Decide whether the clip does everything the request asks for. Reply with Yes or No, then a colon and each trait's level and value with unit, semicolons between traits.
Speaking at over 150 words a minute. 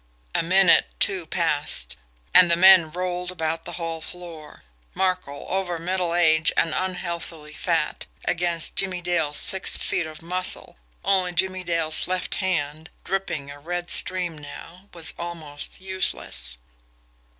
No: slow, 135 wpm